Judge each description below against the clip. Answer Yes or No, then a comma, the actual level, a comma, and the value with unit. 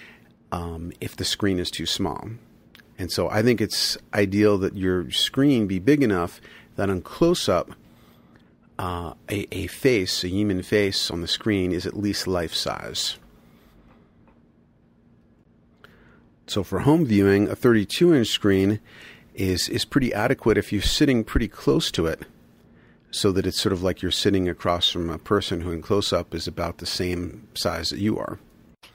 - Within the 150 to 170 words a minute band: Yes, average, 160 wpm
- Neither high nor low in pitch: No, very low, 95 Hz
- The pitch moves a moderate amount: Yes, average, 3.1 semitones